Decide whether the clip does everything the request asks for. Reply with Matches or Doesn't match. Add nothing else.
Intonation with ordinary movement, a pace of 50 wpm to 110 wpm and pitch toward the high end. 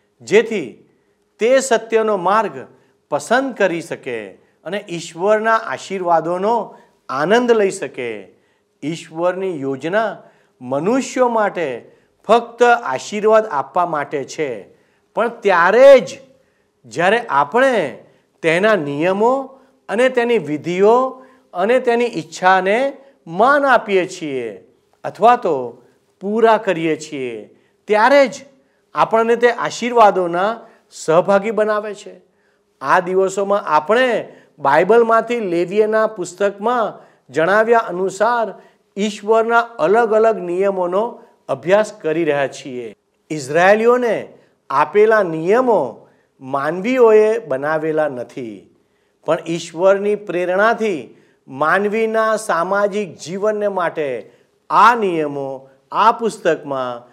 Matches